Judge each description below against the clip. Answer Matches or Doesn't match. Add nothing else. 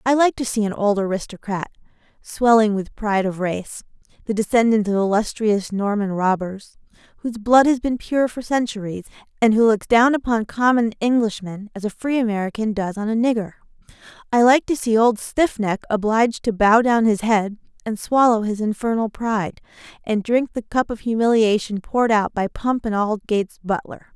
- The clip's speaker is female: Matches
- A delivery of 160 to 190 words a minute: Matches